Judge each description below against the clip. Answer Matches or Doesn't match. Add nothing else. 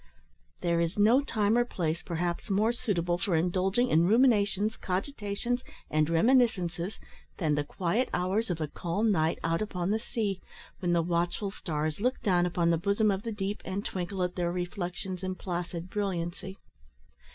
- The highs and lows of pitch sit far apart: Doesn't match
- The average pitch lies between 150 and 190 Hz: Matches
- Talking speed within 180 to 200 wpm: Doesn't match